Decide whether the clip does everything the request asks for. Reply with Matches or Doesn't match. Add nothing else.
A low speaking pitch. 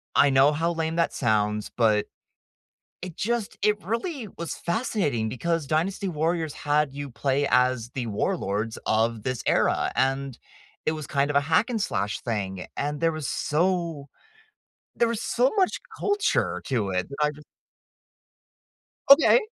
Doesn't match